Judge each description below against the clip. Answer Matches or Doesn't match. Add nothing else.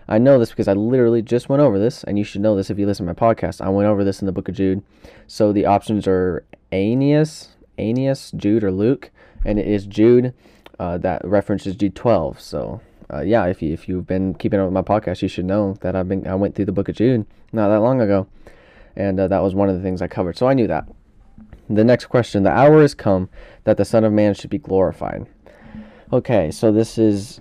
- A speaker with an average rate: Doesn't match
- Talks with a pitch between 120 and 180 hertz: Doesn't match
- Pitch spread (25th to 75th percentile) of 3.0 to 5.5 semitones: Doesn't match